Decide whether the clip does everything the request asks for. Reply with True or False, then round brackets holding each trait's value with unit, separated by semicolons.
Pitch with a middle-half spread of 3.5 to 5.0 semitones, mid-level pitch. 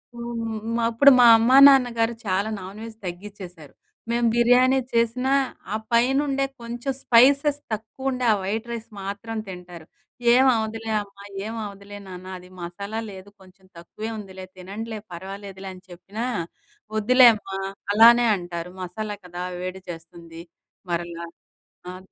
False (4.1 semitones; 210 Hz)